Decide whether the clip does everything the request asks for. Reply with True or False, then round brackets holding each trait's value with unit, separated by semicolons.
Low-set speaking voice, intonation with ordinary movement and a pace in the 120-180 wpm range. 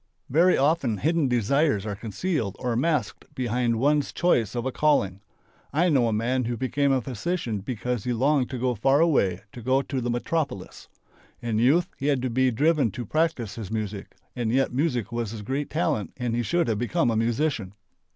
False (125 Hz; 4.3 semitones; 195 wpm)